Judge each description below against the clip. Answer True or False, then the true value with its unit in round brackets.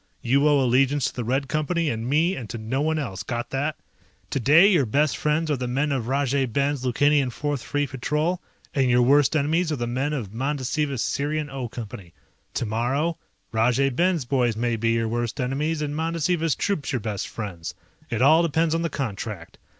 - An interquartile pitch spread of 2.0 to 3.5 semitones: False (4.0 semitones)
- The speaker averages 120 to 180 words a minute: False (190 wpm)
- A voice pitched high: False (135 Hz)